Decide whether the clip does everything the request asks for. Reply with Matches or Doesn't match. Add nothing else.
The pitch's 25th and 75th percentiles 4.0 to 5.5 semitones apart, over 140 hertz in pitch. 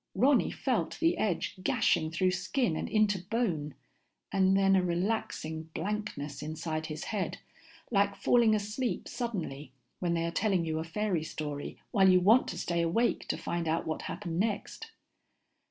Matches